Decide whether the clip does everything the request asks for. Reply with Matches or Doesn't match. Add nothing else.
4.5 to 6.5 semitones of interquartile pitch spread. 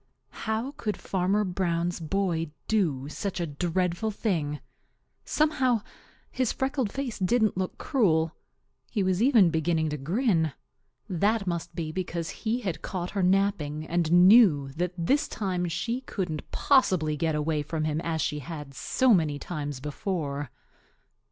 Matches